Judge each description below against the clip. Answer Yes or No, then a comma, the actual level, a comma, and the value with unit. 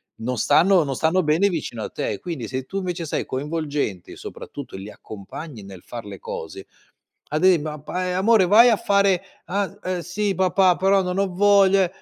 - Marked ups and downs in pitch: Yes, wide, 5.9 semitones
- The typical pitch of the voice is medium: Yes, medium, 175 Hz